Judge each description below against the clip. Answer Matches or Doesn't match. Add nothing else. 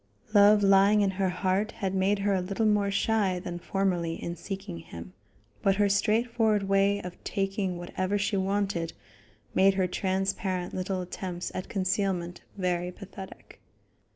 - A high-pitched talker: Matches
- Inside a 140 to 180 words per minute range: Matches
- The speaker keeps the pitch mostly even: Matches